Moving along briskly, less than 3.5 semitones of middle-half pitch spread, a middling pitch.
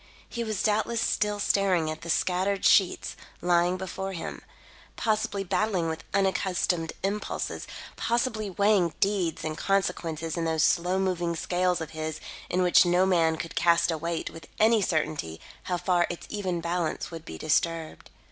No: average, 155 wpm; average, 3.1 semitones; medium, 180 Hz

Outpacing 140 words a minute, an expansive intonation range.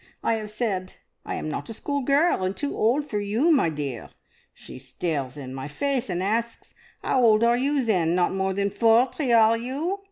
Yes: average, 195 wpm; wide, 5.7 semitones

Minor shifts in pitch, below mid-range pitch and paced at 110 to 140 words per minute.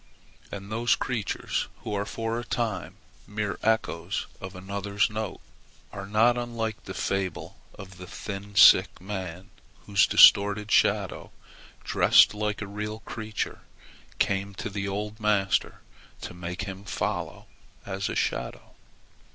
Yes: narrow, 1.9 semitones; low, 100 Hz; slow, 135 wpm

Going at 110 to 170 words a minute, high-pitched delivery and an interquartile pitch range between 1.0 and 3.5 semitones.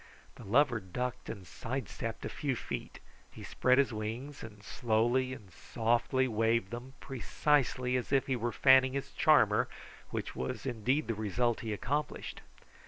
No: average, 160 wpm; low, 120 Hz; average, 2.9 semitones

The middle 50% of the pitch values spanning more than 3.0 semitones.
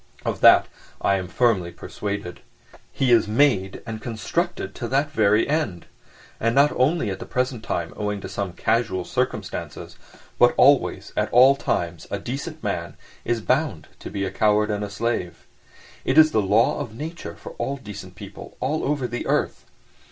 Yes: average, 5.1 semitones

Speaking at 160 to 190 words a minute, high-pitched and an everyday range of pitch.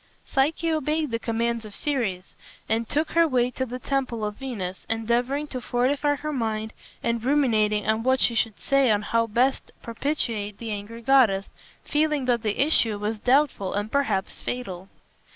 Yes: average, 170 wpm; high, 235 Hz; average, 4.1 semitones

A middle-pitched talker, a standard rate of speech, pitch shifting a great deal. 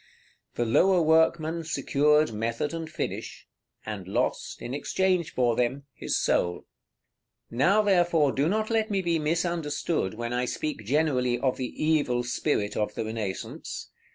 Yes: medium, 150 Hz; average, 155 wpm; wide, 5.7 semitones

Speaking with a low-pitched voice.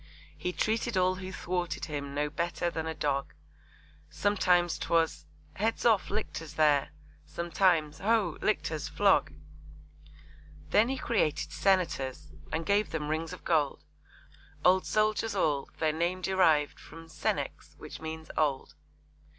No: medium, 170 Hz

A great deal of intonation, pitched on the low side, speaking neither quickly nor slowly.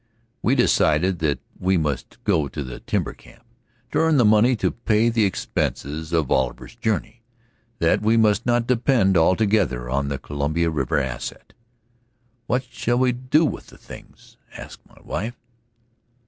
Yes: wide, 7.8 semitones; low, 100 Hz; average, 155 wpm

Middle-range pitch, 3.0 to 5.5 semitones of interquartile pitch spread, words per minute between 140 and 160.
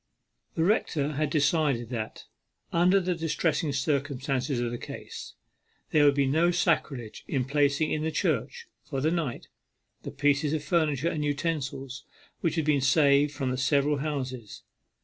No: medium, 145 Hz; narrow, 2.6 semitones; average, 155 wpm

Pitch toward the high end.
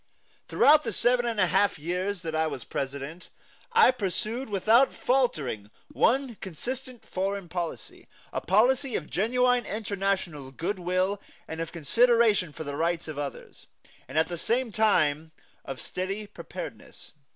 Yes: high, 195 Hz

